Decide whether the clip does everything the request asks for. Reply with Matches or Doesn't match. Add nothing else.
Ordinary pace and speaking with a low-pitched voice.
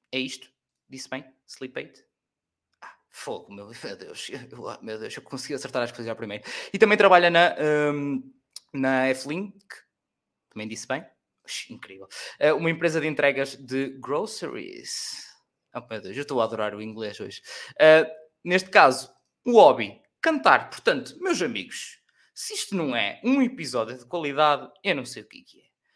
Doesn't match